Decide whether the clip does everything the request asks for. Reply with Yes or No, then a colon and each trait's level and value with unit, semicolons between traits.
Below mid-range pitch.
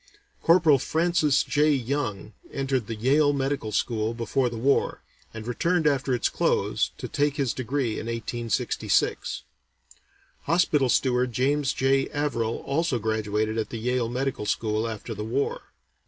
Yes: low, 130 Hz